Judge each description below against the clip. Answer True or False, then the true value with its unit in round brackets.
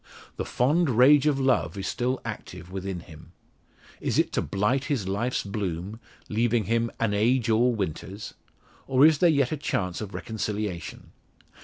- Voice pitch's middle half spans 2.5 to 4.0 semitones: False (4.9 semitones)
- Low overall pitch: True (110 Hz)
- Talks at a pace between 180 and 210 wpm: False (160 wpm)